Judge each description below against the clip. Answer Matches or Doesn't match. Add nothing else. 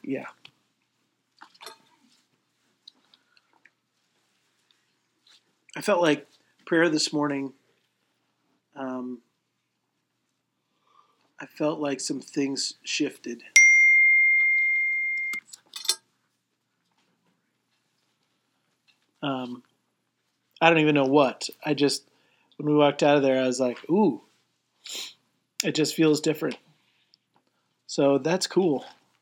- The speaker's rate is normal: Doesn't match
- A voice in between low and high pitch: Matches